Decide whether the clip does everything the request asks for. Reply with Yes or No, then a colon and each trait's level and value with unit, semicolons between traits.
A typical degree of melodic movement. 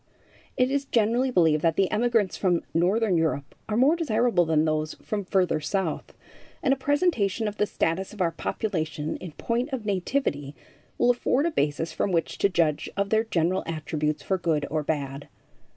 No: wide, 6.4 semitones